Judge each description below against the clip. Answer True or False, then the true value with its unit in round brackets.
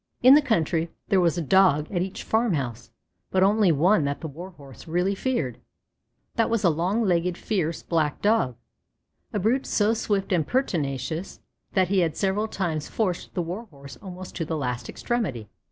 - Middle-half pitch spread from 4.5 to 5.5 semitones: True (4.8 semitones)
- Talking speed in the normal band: True (175 wpm)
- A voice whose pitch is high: False (180 Hz)